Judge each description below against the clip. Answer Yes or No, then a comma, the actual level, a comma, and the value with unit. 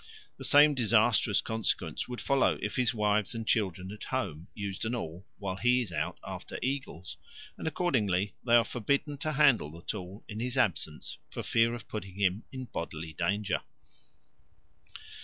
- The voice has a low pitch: Yes, low, 110 Hz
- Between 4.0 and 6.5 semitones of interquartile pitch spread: Yes, average, 4.8 semitones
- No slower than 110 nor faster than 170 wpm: Yes, average, 165 wpm